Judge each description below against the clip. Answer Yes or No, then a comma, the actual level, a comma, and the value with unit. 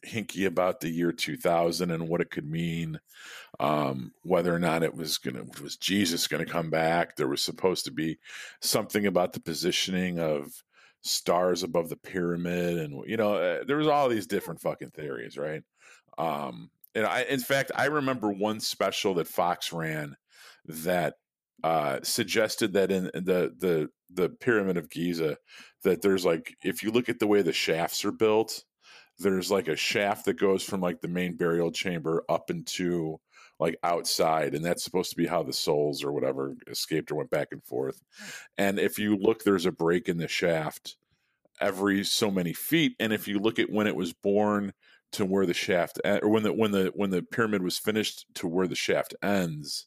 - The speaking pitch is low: Yes, very low, 90 Hz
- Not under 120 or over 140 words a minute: No, average, 190 wpm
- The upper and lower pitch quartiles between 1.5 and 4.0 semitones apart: Yes, average, 3.5 semitones